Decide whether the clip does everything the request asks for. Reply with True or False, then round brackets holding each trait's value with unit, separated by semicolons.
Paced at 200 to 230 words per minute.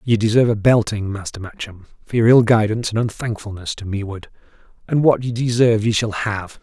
False (190 wpm)